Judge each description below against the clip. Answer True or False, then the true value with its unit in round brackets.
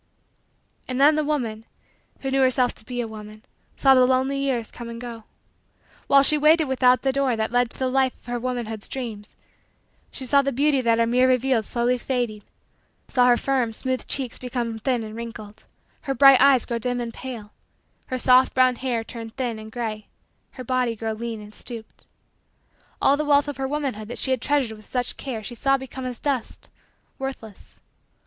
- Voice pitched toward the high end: True (250 Hz)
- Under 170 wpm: False (195 wpm)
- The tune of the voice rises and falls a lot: False (2.6 semitones)